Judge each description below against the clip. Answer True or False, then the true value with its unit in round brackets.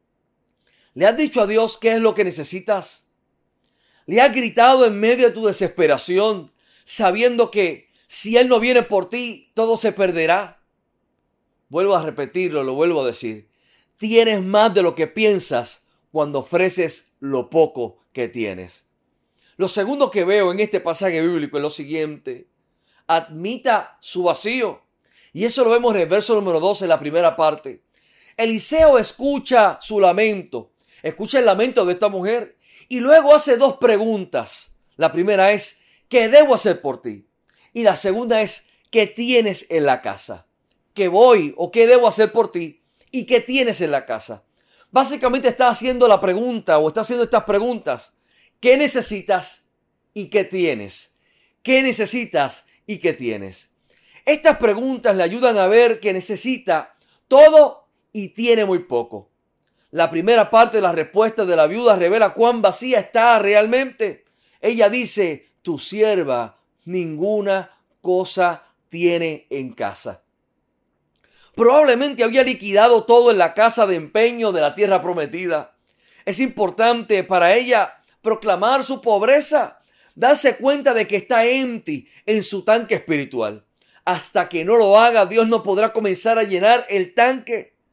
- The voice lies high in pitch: True (215 Hz)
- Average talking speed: True (150 wpm)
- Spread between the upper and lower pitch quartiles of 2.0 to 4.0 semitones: False (5.2 semitones)